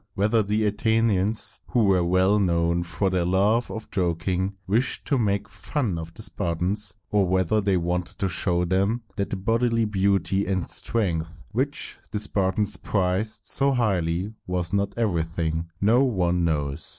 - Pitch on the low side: Yes, very low, 95 Hz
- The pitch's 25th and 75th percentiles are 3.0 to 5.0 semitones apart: Yes, average, 3.4 semitones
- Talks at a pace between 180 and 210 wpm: No, average, 160 wpm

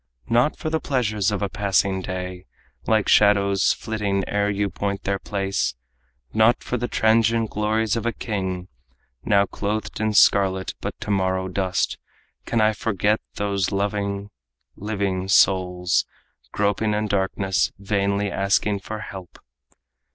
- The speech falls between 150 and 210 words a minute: No, slow, 135 wpm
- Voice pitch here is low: Yes, low, 100 Hz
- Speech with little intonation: Yes, narrow, 1.8 semitones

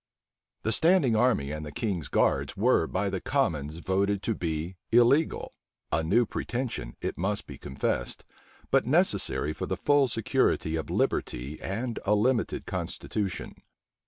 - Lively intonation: Yes, wide, 7.1 semitones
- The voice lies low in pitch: Yes, low, 100 Hz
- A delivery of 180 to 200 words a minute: No, average, 145 wpm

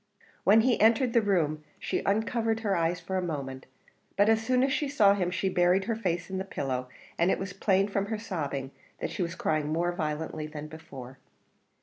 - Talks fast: Yes, fast, 210 wpm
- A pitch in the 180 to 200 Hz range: Yes, medium, 185 Hz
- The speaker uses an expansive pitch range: Yes, wide, 5.8 semitones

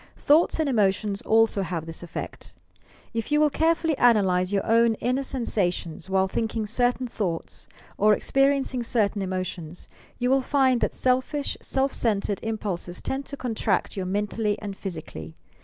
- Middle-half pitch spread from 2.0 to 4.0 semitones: No, average, 5.2 semitones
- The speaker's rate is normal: Yes, average, 155 wpm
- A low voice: No, high, 220 Hz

